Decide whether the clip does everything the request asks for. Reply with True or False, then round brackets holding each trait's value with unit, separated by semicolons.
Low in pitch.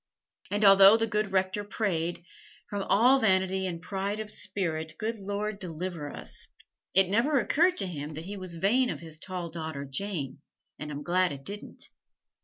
False (190 Hz)